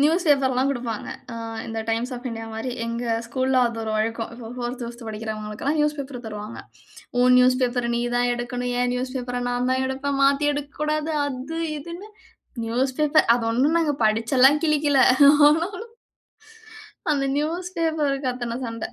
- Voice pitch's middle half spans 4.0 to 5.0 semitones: No, average, 3.6 semitones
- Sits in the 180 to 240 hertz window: No, very high, 255 Hz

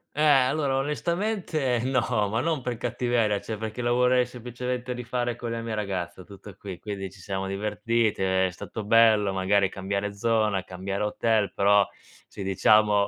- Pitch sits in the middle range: No, low, 110 Hz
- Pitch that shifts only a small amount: No, average, 3.7 semitones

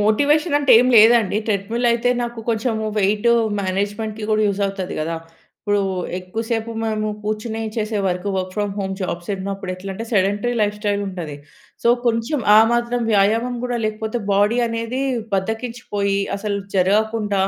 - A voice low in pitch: No, high, 215 Hz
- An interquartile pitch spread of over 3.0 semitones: No, average, 2.7 semitones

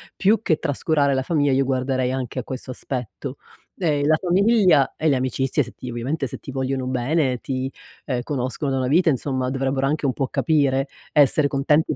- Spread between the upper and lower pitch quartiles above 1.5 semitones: Yes, narrow, 2.6 semitones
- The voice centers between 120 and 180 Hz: Yes, low, 135 Hz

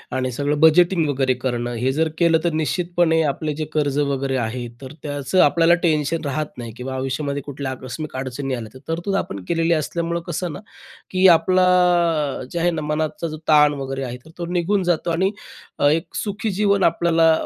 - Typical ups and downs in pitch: Yes, average, 4.1 semitones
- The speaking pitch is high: No, medium, 155 Hz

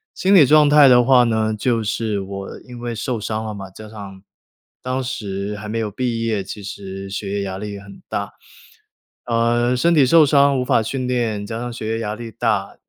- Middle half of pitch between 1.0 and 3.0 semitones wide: No, average, 3.6 semitones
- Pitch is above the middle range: No, low, 115 Hz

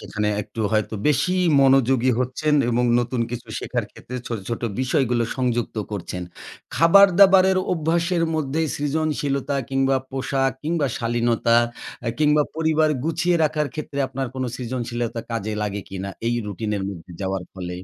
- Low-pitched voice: Yes, low, 130 Hz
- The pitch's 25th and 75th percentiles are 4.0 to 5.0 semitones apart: Yes, average, 4.7 semitones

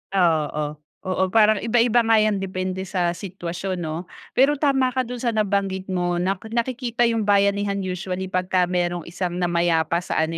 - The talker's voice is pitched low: No, high, 190 Hz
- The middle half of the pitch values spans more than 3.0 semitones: Yes, average, 3.6 semitones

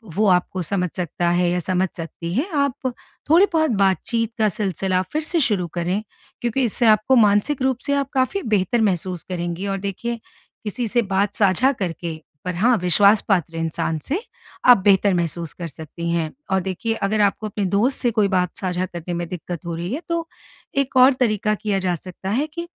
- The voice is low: No, high, 195 Hz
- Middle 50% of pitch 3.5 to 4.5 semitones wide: No, average, 5.0 semitones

